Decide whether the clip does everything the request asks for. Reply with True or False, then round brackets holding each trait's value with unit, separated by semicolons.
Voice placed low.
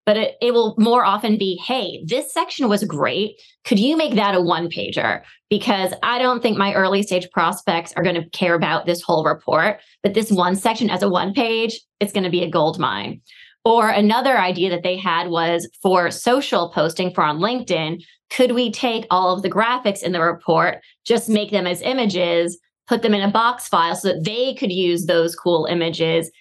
False (195 Hz)